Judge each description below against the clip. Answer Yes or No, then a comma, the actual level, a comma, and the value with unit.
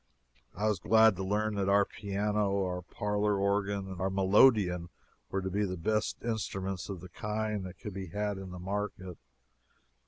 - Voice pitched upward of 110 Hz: No, low, 100 Hz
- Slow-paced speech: No, average, 180 wpm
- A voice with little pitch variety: Yes, narrow, 1.8 semitones